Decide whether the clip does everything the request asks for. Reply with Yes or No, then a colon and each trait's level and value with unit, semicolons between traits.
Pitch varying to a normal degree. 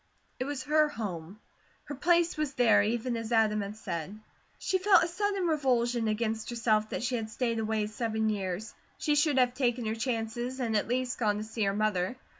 Yes: average, 3.2 semitones